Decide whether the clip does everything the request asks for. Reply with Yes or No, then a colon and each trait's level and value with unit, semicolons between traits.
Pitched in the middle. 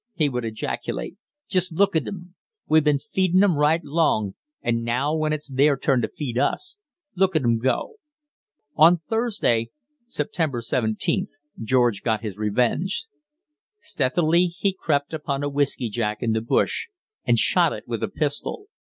Yes: medium, 145 Hz